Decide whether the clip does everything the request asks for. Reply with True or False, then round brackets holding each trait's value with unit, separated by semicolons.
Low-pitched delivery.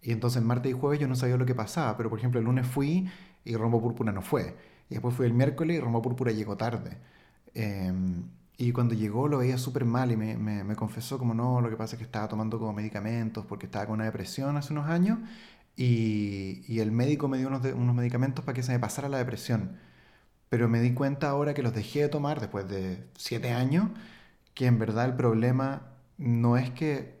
True (120 Hz)